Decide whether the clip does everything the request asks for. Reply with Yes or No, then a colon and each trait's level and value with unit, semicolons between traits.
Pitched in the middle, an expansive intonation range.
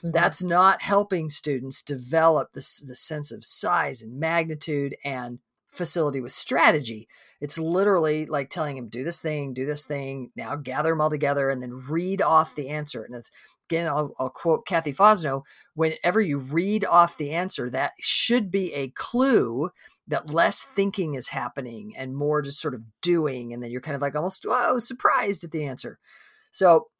No: medium, 150 Hz; average, 4.2 semitones